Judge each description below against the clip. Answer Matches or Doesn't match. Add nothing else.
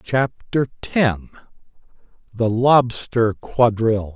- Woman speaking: Doesn't match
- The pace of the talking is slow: Matches